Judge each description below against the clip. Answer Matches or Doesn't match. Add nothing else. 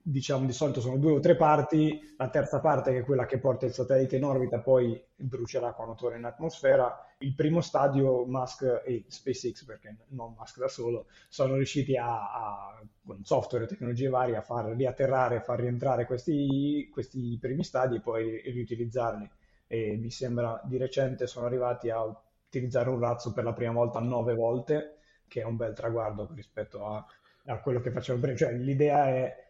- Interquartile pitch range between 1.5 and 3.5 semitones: Matches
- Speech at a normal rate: Doesn't match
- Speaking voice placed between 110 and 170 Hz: Matches